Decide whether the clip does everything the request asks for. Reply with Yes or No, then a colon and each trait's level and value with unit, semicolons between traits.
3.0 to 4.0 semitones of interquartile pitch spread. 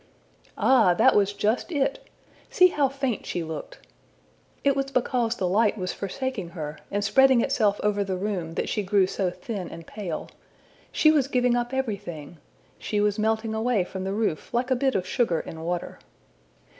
No: wide, 5.5 semitones